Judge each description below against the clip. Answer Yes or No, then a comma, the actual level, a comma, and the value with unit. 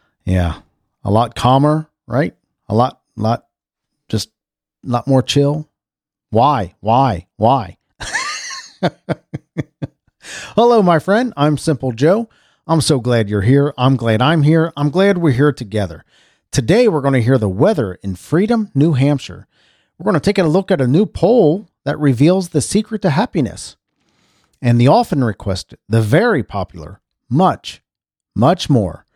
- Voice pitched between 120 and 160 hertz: Yes, medium, 140 Hz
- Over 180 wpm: No, average, 150 wpm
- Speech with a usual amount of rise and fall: No, wide, 6.1 semitones